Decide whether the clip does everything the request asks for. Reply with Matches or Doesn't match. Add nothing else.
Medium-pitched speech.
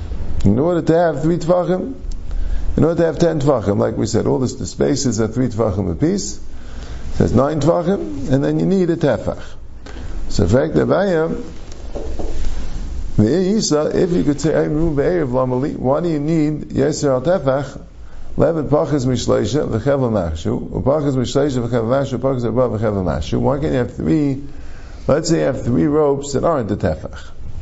Doesn't match